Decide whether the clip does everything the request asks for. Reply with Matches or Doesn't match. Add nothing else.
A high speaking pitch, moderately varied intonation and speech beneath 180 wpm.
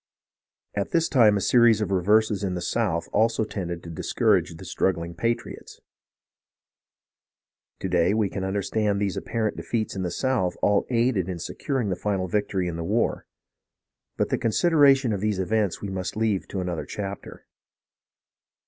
Doesn't match